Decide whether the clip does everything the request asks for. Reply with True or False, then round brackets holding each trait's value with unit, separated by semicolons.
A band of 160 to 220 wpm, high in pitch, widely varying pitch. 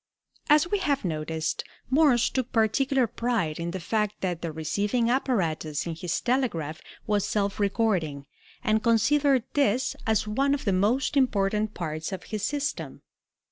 False (150 wpm; 215 Hz; 6.6 semitones)